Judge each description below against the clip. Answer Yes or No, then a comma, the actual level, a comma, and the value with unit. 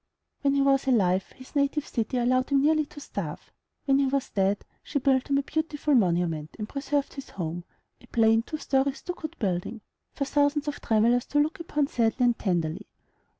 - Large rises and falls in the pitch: No, average, 4.5 semitones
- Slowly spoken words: No, average, 190 wpm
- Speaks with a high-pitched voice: Yes, very high, 265 Hz